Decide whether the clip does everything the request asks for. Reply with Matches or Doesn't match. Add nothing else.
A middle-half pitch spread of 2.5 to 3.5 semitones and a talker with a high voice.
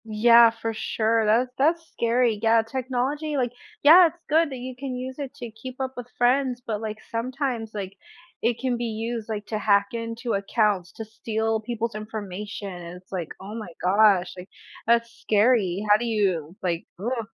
Matches